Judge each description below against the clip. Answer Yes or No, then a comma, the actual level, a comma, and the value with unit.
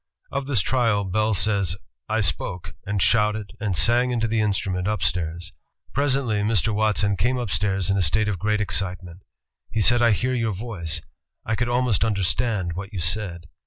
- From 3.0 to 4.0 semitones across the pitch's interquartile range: Yes, average, 3.4 semitones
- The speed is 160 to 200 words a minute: Yes, average, 175 wpm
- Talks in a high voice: No, low, 105 Hz